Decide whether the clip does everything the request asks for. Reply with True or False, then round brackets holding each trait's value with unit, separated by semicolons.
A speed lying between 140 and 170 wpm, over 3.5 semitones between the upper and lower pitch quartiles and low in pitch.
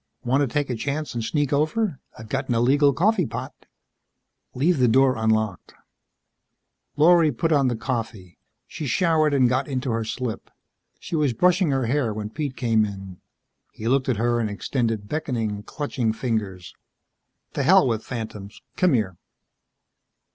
True (160 wpm; 4.6 semitones; 125 Hz)